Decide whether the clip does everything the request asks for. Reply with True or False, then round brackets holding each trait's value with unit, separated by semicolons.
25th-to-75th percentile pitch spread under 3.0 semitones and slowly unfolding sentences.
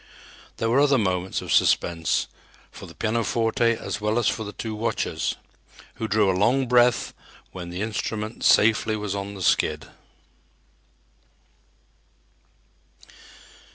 True (2.6 semitones; 125 wpm)